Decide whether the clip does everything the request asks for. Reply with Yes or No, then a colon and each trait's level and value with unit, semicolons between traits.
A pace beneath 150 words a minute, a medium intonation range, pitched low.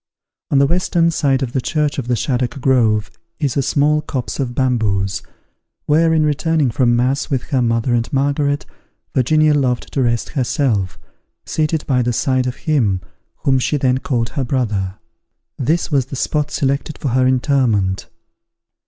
No: average, 165 wpm; average, 3.2 semitones; low, 130 Hz